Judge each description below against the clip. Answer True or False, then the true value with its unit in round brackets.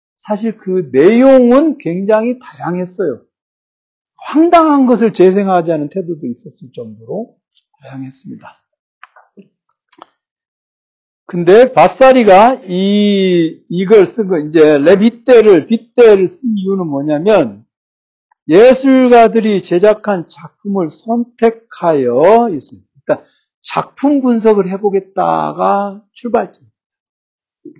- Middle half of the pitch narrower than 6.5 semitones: True (6.0 semitones)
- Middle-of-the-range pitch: False (200 Hz)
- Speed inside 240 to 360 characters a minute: False (220 characters per minute)